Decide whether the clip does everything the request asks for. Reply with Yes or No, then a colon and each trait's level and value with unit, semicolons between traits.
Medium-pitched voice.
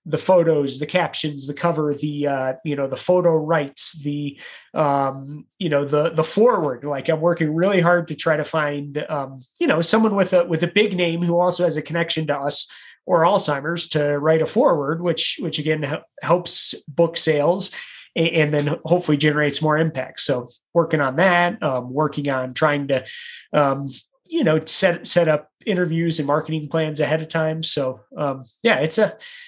Yes: medium, 155 Hz